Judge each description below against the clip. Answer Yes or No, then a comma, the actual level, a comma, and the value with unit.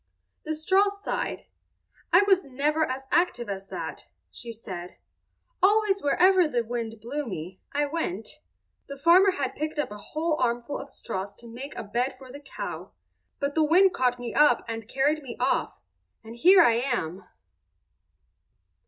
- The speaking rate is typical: Yes, average, 160 wpm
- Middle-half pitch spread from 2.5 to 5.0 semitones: No, wide, 5.4 semitones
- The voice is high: Yes, very high, 275 Hz